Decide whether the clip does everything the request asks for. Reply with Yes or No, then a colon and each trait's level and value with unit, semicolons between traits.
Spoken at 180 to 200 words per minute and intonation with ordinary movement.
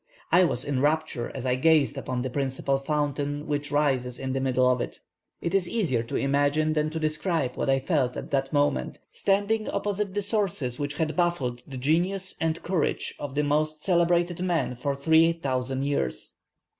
Yes: average, 185 wpm; average, 4.0 semitones